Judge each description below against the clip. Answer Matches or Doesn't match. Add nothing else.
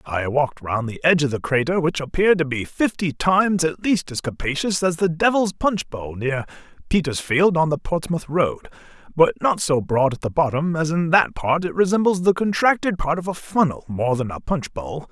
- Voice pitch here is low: Doesn't match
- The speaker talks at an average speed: Doesn't match